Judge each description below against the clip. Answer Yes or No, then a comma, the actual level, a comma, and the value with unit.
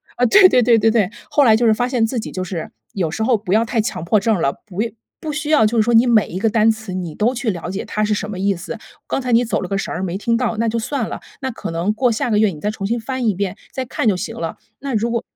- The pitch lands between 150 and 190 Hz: No, high, 220 Hz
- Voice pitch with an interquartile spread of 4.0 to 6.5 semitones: No, average, 3.3 semitones